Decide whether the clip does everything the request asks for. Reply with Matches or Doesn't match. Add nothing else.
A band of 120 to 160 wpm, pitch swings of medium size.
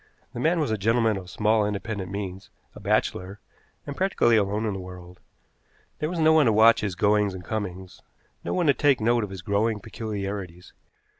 Doesn't match